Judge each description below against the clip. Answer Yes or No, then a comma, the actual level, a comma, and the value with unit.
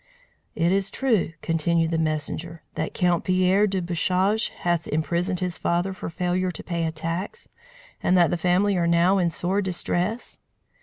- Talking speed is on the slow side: No, average, 165 wpm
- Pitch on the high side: No, medium, 175 Hz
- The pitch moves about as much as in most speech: No, narrow, 1.9 semitones